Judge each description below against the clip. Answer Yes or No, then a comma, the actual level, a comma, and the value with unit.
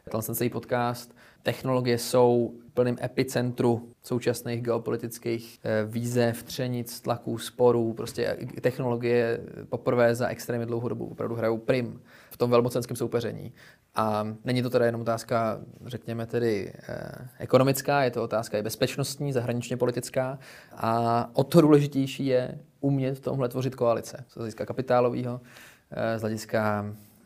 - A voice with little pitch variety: Yes, narrow, 1.5 semitones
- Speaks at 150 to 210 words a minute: No, average, 135 wpm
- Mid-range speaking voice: No, low, 120 Hz